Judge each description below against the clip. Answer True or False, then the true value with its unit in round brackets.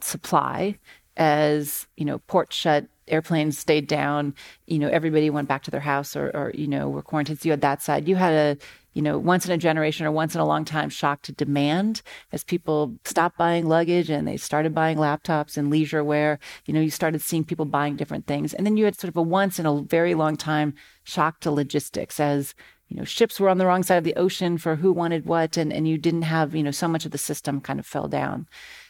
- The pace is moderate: False (240 wpm)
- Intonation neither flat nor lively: False (2.2 semitones)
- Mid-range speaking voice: True (155 Hz)